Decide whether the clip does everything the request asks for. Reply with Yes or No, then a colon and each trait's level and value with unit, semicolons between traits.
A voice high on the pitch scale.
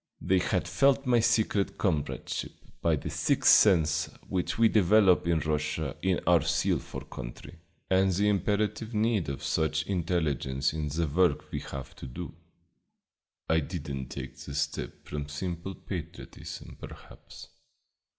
No: very low, 85 Hz